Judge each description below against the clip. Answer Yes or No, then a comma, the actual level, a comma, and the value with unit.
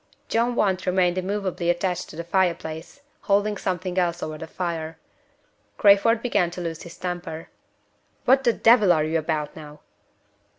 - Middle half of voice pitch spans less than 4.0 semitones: Yes, average, 3.4 semitones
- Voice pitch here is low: No, medium, 180 Hz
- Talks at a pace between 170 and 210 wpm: No, average, 160 wpm